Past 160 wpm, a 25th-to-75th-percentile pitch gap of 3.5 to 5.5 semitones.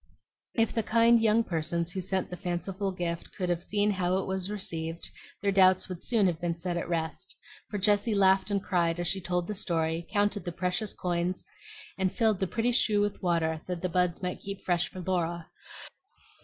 No: average, 200 wpm; average, 2.8 semitones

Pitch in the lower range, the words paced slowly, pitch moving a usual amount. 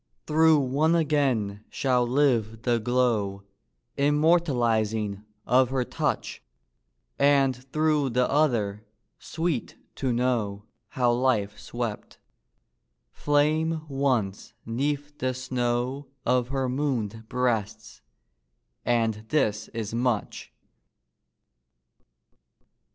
Yes: low, 125 Hz; slow, 90 wpm; average, 4.1 semitones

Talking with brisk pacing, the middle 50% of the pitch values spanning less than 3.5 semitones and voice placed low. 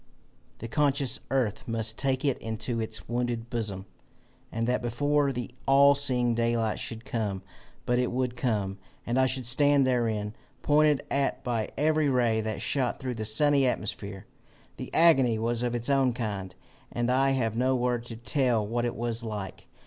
No: average, 170 wpm; average, 3.0 semitones; low, 120 Hz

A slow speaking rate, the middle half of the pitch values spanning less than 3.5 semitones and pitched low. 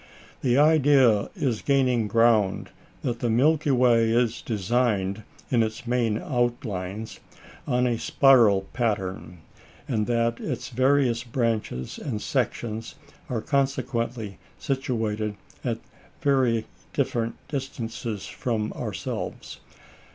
Yes: slow, 105 wpm; average, 2.8 semitones; low, 115 Hz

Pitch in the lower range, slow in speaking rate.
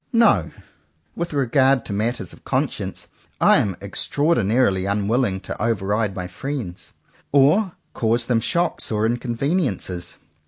Yes: low, 115 Hz; slow, 130 wpm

